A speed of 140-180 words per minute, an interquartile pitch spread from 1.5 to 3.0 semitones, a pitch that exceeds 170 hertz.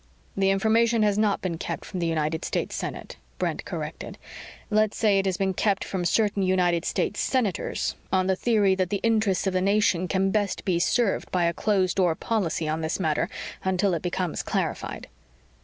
No: average, 190 wpm; average, 2.7 semitones; high, 190 Hz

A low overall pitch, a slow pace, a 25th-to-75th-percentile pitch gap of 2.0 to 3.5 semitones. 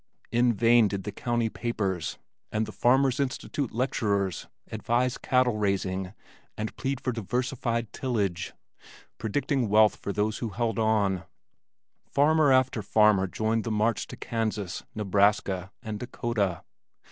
Yes: low, 110 Hz; slow, 125 wpm; average, 3.2 semitones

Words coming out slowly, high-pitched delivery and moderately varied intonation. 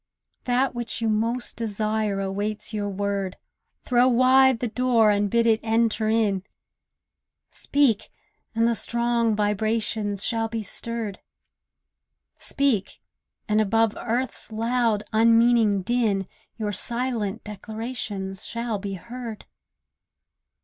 No: slow, 110 wpm; high, 225 Hz; narrow, 2.2 semitones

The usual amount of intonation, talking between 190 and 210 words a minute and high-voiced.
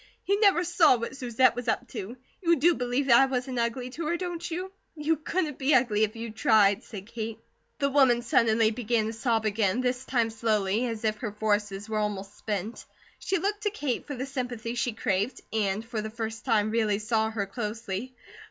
Yes: average, 3.4 semitones; fast, 205 wpm; high, 235 Hz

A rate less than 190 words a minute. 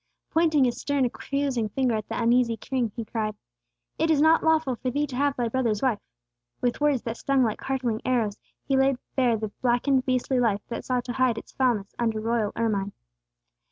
No: average, 195 wpm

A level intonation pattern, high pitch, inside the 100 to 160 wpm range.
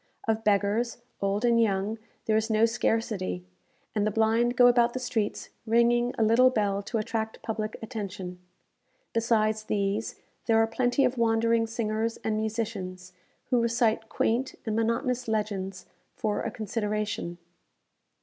Yes: narrow, 1.7 semitones; high, 220 Hz; average, 140 wpm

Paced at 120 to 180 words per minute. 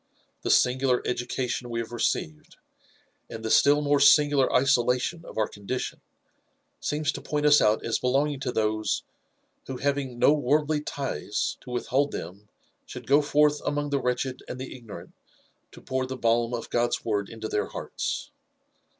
Yes: average, 165 wpm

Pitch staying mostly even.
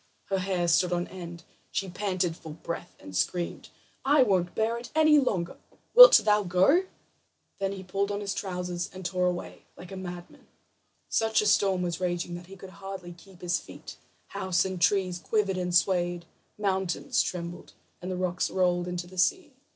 Yes: narrow, 2.0 semitones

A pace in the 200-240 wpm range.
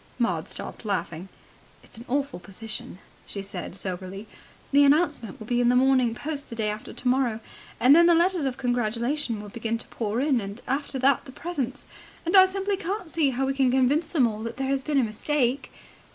Yes: fast, 205 wpm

